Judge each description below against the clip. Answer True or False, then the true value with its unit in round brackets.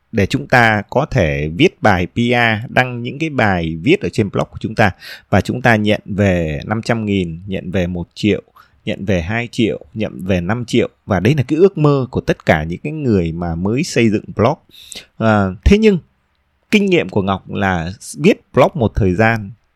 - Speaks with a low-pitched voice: True (105 Hz)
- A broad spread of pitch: False (4.8 semitones)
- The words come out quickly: False (205 wpm)